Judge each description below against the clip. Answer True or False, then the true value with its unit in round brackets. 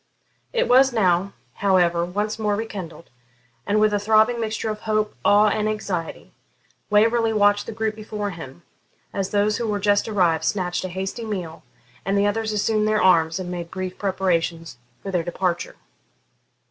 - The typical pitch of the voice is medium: False (205 Hz)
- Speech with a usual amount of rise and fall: True (3.2 semitones)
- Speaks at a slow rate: False (165 wpm)